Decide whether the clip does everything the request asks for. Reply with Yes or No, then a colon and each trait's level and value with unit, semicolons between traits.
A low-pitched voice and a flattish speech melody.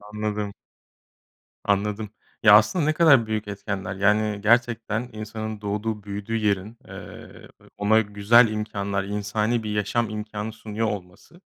Yes: low, 105 Hz; narrow, 1.4 semitones